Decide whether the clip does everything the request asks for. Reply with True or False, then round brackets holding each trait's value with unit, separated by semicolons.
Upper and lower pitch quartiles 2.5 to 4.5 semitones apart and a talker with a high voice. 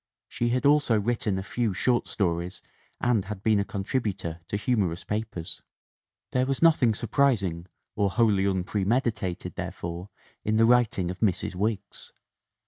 False (4.0 semitones; 105 Hz)